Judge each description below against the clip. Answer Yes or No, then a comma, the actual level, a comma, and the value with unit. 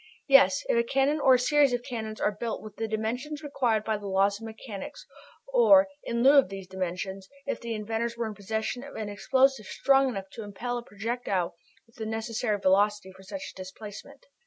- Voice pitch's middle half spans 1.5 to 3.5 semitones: No, average, 4.1 semitones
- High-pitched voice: Yes, high, 225 Hz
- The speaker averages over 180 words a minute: Yes, fast, 205 wpm